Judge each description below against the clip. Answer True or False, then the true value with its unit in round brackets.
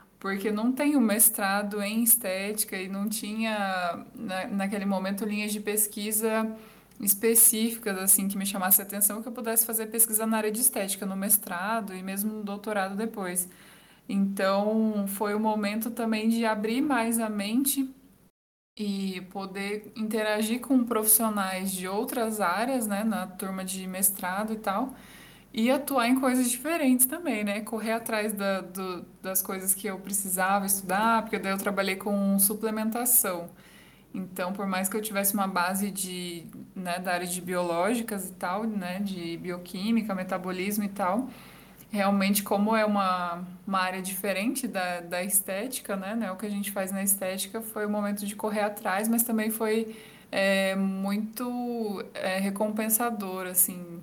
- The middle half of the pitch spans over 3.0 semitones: False (2.5 semitones)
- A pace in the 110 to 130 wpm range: False (155 wpm)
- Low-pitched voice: False (205 Hz)